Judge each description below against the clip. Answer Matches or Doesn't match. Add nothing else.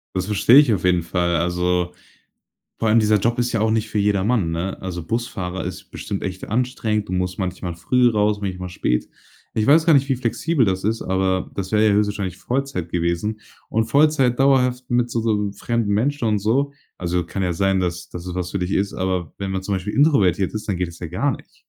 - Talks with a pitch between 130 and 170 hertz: Doesn't match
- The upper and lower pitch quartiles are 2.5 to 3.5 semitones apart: Doesn't match